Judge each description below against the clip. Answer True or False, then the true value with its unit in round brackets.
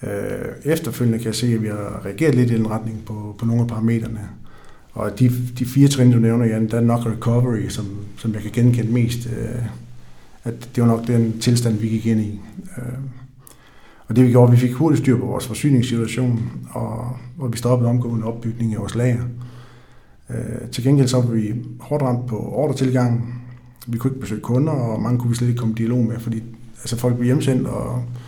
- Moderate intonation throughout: False (1.6 semitones)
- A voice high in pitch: False (120 Hz)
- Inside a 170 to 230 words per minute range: True (215 wpm)